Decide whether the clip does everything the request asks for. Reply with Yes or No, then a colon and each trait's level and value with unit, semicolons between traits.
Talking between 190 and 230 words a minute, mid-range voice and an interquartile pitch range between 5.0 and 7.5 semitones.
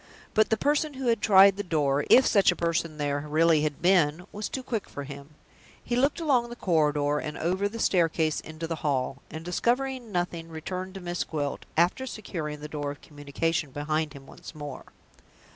Yes: average, 195 wpm; medium, 165 Hz; wide, 5.4 semitones